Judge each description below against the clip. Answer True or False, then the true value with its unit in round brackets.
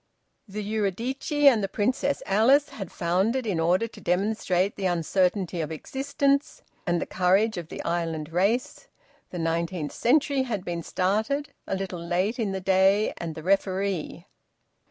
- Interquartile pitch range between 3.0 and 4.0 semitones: False (4.6 semitones)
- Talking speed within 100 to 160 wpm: True (155 wpm)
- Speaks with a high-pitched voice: True (195 Hz)